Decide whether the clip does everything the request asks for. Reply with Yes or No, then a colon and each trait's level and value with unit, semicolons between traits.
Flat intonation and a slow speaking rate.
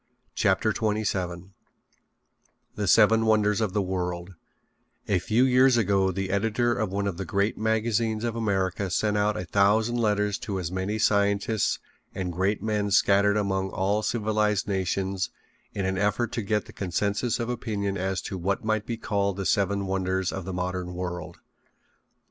No: narrow, 2.3 semitones; average, 165 wpm